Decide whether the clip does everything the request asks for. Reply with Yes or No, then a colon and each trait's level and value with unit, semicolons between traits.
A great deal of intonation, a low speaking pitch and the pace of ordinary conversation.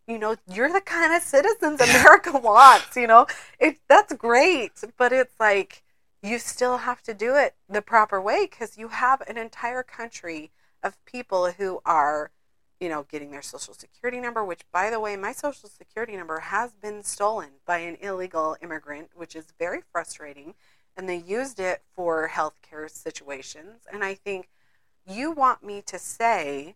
No: wide, 6.1 semitones; high, 210 Hz; average, 175 wpm